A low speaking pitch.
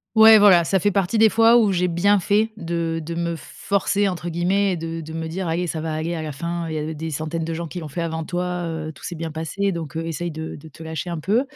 No: medium, 170 Hz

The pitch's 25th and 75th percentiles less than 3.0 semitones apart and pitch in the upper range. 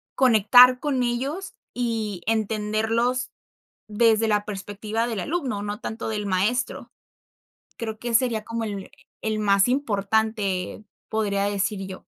Yes: narrow, 2.6 semitones; high, 220 Hz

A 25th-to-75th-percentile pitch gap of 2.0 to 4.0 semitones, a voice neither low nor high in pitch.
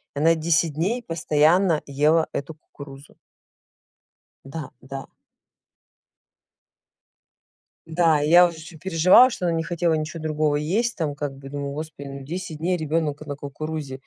Yes: narrow, 2.5 semitones; medium, 155 Hz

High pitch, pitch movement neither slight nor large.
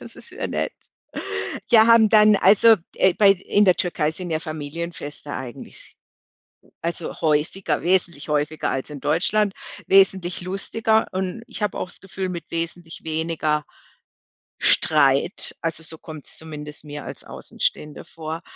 No: medium, 170 Hz; average, 4.0 semitones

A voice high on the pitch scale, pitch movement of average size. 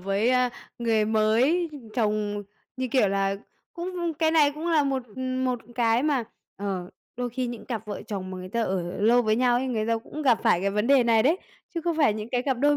Yes: high, 235 Hz; average, 4.4 semitones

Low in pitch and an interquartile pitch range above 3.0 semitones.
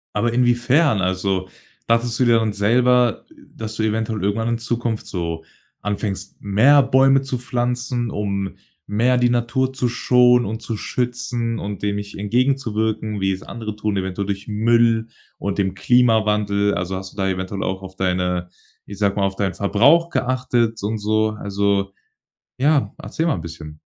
Yes: low, 110 Hz; average, 3.5 semitones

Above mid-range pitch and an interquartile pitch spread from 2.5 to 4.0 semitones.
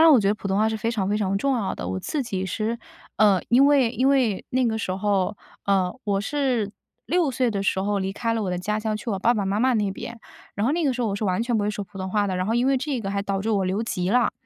Yes: high, 215 Hz; average, 3.5 semitones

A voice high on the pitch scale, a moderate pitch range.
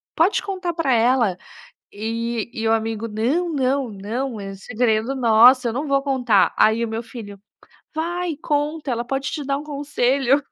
Yes: very high, 250 Hz; average, 4.1 semitones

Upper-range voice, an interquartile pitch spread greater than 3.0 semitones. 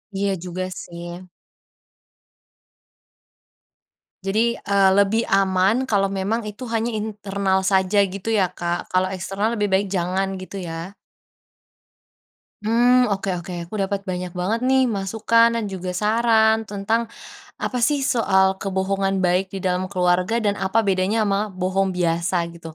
No: high, 195 Hz; narrow, 2.4 semitones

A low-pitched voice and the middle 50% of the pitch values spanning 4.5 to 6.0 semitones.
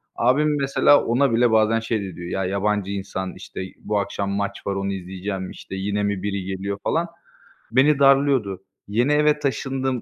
Yes: low, 105 Hz; wide, 5.4 semitones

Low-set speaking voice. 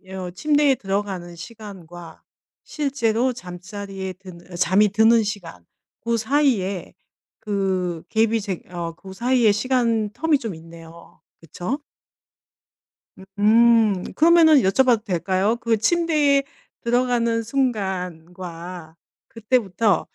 No: high, 210 Hz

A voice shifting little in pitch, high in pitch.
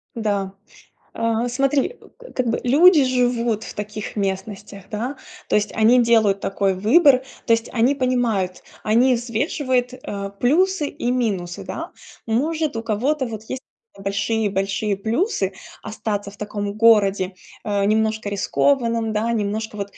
No: average, 3.7 semitones; high, 225 Hz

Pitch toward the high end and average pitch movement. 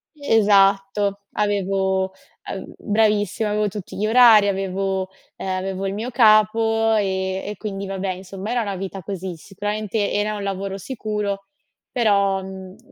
No: high, 200 Hz; narrow, 1.8 semitones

